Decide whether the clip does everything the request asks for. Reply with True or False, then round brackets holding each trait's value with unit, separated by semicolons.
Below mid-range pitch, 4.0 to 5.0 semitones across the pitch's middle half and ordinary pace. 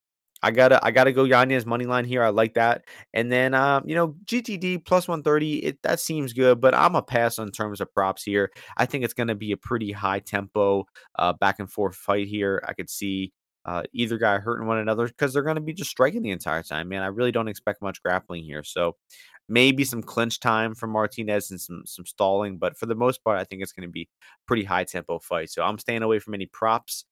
False (110 Hz; 4.5 semitones; 250 wpm)